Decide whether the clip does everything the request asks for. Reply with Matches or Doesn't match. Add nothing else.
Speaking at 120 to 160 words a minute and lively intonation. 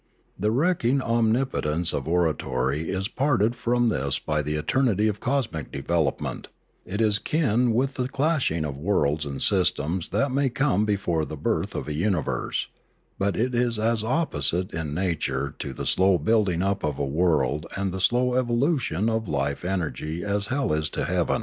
Doesn't match